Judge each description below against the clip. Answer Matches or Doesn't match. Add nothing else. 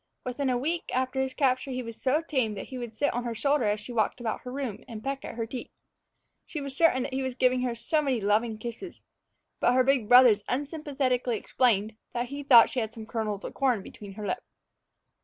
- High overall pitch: Matches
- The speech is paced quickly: Matches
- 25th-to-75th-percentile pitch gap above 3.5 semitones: Doesn't match